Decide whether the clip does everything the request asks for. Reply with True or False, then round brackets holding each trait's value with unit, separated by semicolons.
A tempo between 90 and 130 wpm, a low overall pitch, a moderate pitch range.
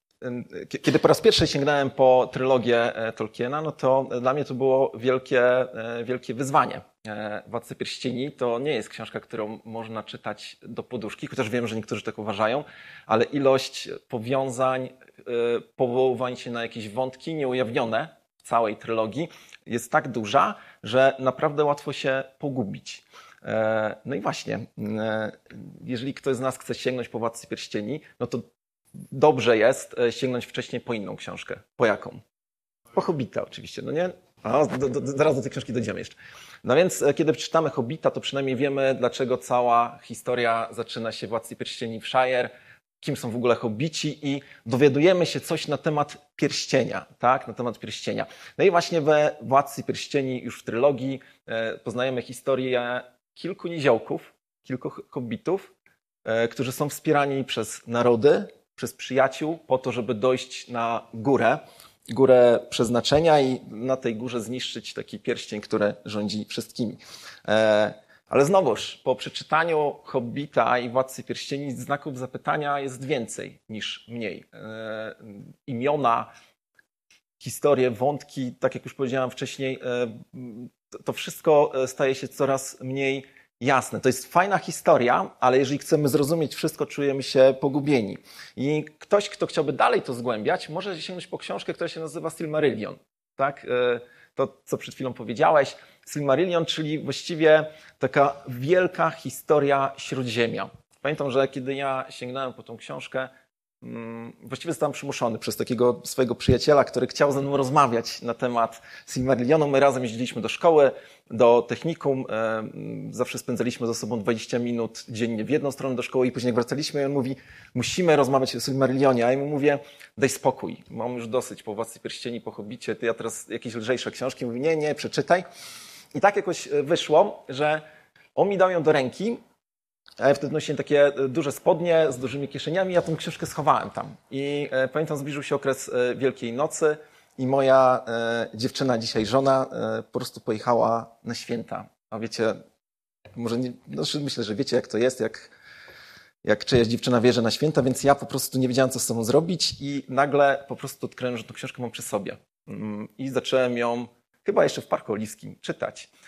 False (155 wpm; 130 Hz; 3.1 semitones)